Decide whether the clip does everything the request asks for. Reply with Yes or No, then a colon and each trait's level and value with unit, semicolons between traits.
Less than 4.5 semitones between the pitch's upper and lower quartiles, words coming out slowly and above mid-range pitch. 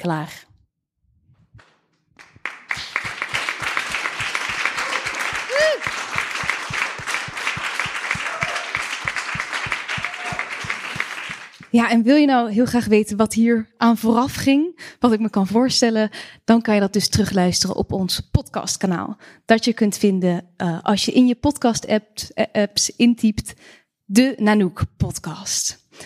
Yes: average, 2.9 semitones; slow, 100 wpm; high, 225 Hz